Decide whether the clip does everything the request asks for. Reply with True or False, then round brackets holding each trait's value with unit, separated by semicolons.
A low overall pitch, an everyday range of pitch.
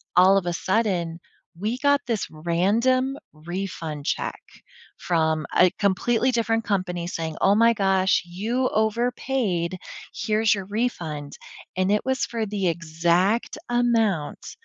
False (195 Hz; 5.0 semitones)